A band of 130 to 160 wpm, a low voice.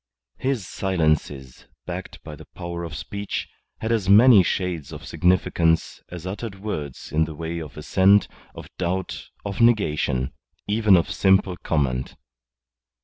Yes: average, 140 wpm; very low, 90 Hz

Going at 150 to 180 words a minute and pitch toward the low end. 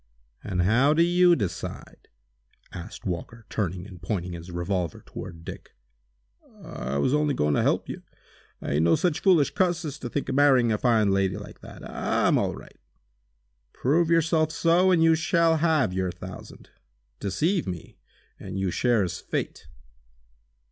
Yes: average, 160 wpm; low, 115 Hz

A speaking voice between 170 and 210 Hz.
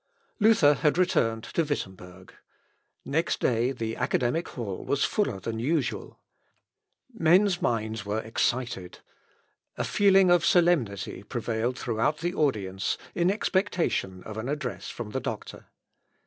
No: low, 125 Hz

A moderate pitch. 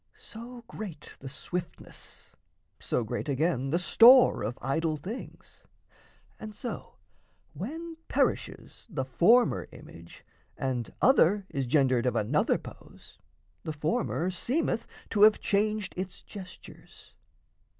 Yes: medium, 175 Hz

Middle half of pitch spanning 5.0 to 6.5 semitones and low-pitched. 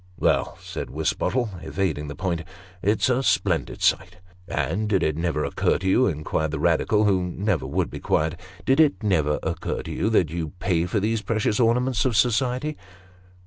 Yes: wide, 5.5 semitones; very low, 95 Hz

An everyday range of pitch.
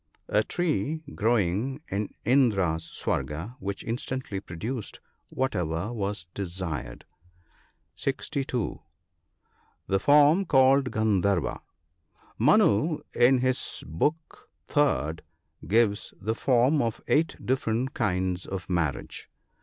No: wide, 6.0 semitones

